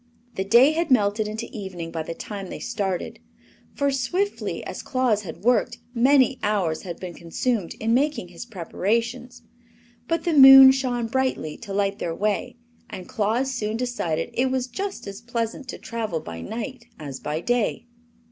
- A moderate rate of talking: Yes, average, 165 wpm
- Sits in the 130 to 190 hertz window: No, high, 230 Hz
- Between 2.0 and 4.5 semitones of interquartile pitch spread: No, average, 5.0 semitones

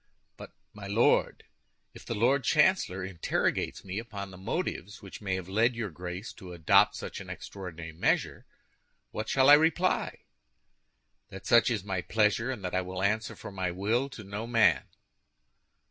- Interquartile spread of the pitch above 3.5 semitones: Yes, average, 3.9 semitones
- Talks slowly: No, average, 160 wpm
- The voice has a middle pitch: No, low, 100 Hz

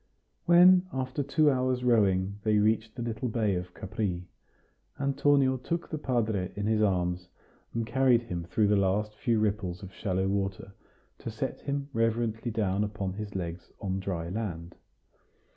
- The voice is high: No, low, 105 Hz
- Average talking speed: Yes, average, 160 wpm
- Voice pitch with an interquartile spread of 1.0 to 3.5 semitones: No, average, 4.5 semitones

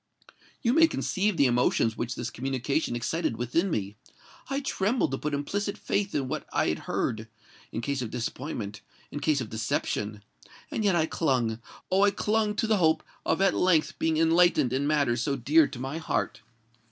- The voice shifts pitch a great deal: Yes, wide, 6.9 semitones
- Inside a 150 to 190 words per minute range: Yes, average, 170 wpm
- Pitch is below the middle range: No, medium, 145 Hz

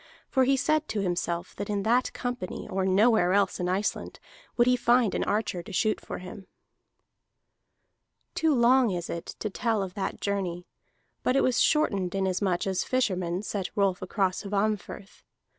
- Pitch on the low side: No, high, 200 Hz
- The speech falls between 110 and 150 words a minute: No, average, 165 wpm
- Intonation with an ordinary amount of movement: Yes, average, 4.5 semitones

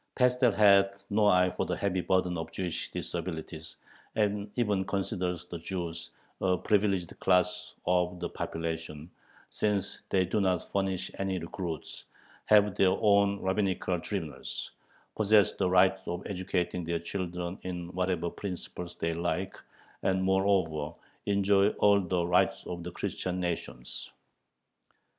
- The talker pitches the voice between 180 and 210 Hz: No, very low, 95 Hz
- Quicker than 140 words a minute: No, slow, 135 wpm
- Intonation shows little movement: Yes, narrow, 2.3 semitones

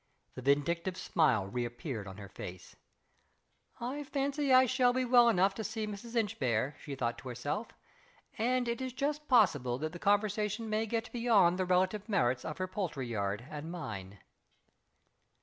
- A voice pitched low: No, medium, 185 Hz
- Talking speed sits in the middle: Yes, average, 165 wpm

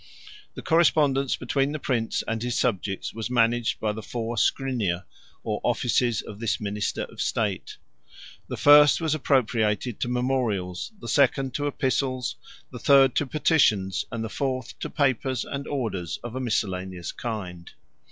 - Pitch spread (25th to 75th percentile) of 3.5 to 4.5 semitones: Yes, average, 4.1 semitones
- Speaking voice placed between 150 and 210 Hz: No, low, 120 Hz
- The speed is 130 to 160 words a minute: Yes, average, 150 wpm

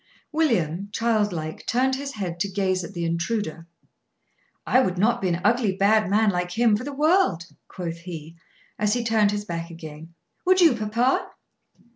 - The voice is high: Yes, high, 205 Hz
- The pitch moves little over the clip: No, wide, 5.4 semitones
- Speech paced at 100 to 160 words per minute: No, average, 175 wpm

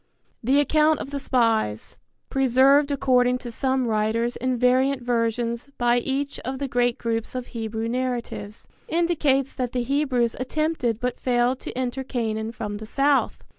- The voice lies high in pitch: Yes, very high, 250 Hz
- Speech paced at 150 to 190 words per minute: Yes, average, 155 wpm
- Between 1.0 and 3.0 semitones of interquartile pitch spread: Yes, narrow, 2.6 semitones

